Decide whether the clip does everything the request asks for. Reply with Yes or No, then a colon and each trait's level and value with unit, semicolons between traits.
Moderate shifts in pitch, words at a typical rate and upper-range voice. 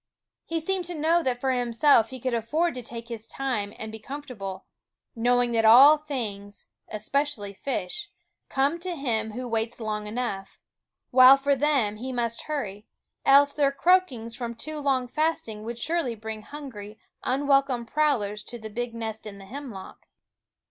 Yes: average, 4.4 semitones; average, 160 wpm; high, 245 Hz